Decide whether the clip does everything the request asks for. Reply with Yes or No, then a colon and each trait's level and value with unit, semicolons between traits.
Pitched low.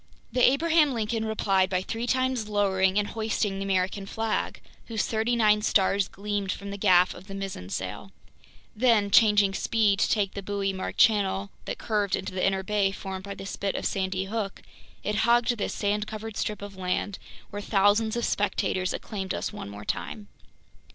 No: high, 205 Hz